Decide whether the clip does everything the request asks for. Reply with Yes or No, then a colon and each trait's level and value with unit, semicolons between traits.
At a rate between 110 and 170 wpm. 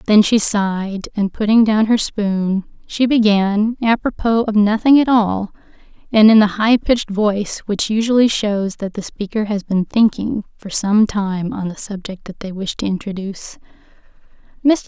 Yes: average, 165 wpm